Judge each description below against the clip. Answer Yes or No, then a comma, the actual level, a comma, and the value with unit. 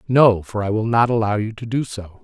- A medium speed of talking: No, fast, 270 wpm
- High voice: No, low, 110 Hz